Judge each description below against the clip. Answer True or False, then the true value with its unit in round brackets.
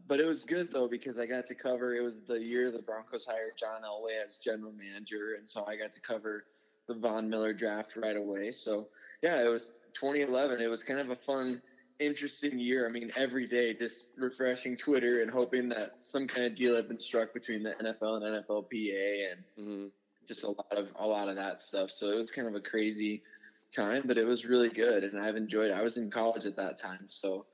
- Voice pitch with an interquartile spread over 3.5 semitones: False (2.8 semitones)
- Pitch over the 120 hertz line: False (115 Hz)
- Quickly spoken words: True (225 wpm)